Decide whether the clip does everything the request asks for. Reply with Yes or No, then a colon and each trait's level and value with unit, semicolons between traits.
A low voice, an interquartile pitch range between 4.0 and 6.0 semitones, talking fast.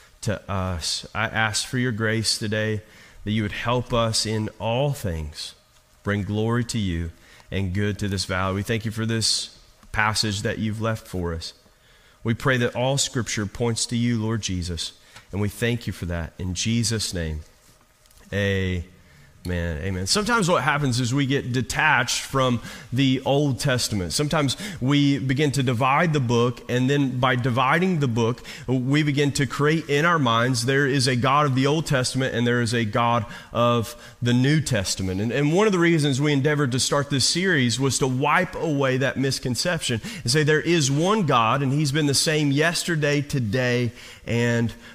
No: low, 120 Hz; average, 4.7 semitones; average, 185 wpm